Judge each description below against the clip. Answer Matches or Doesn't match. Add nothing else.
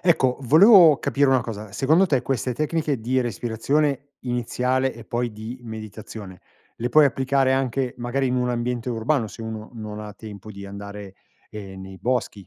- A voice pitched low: Matches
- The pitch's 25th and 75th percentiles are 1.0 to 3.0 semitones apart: Doesn't match